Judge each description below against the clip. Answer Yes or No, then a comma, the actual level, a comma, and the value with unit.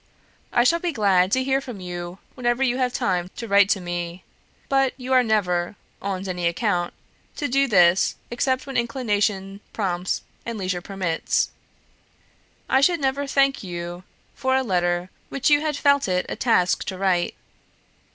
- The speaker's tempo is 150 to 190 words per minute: Yes, average, 165 wpm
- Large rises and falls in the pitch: Yes, wide, 6.5 semitones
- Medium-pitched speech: No, high, 205 Hz